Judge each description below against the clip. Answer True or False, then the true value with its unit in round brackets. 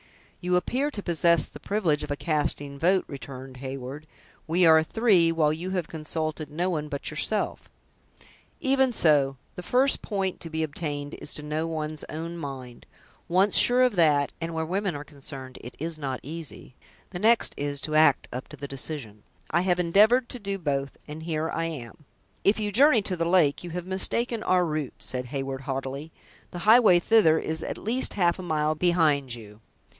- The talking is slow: False (190 wpm)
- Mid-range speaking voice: True (160 Hz)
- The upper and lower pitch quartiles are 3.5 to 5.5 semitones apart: True (4.3 semitones)